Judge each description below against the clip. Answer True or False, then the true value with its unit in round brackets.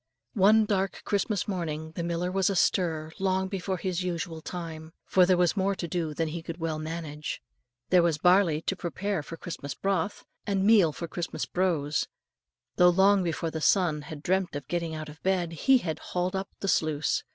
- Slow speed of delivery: False (190 wpm)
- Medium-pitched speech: True (175 Hz)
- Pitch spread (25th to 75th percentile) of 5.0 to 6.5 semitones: False (3.1 semitones)